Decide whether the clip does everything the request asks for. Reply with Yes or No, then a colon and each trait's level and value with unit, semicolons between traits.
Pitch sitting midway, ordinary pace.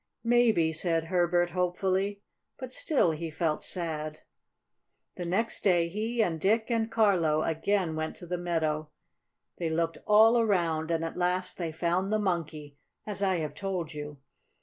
Yes: medium, 175 Hz; average, 155 wpm